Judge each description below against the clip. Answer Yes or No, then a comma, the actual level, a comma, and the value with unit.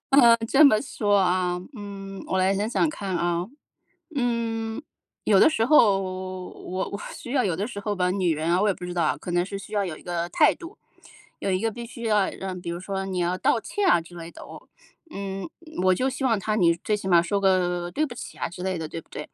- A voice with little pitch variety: No, average, 3.9 semitones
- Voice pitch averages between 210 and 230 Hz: No, high, 195 Hz